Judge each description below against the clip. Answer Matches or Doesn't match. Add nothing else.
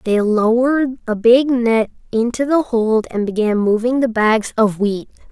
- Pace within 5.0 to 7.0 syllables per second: Doesn't match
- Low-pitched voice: Doesn't match